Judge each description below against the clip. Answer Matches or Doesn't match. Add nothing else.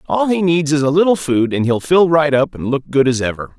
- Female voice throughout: Doesn't match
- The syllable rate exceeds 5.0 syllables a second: Matches